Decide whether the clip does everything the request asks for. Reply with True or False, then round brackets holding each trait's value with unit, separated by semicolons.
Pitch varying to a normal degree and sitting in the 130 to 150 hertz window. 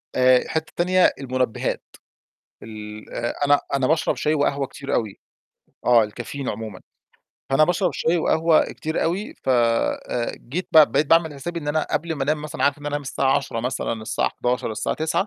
True (4.4 semitones; 140 Hz)